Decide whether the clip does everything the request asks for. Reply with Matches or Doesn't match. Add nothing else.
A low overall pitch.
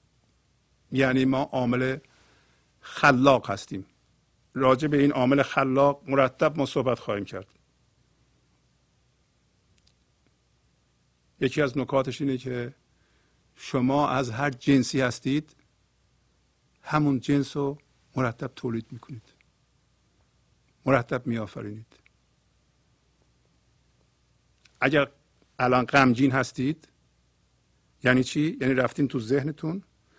Matches